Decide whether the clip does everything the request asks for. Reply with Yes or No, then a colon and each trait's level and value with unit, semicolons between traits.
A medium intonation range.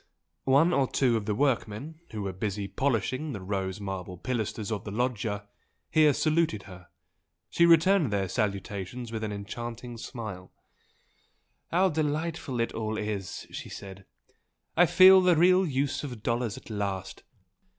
No: wide, 6.3 semitones